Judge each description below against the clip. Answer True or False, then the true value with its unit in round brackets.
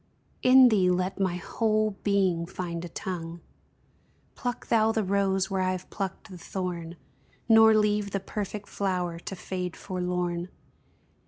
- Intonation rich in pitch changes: False (2.7 semitones)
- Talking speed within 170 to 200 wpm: False (145 wpm)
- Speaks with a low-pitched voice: False (190 Hz)